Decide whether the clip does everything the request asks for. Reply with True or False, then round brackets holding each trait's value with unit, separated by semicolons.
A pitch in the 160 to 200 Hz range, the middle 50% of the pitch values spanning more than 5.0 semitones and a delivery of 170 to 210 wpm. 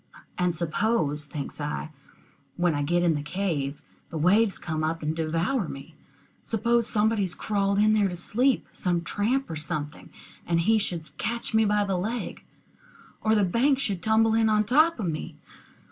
True (190 Hz; 5.5 semitones; 175 wpm)